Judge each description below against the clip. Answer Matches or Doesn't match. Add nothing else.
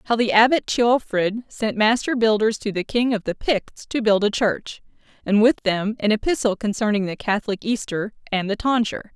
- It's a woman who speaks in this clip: Matches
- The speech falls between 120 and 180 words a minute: Doesn't match